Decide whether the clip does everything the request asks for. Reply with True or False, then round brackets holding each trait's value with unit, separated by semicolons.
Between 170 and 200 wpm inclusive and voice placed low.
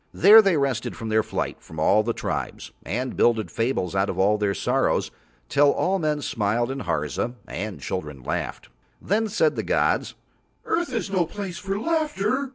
True (175 wpm; 130 Hz)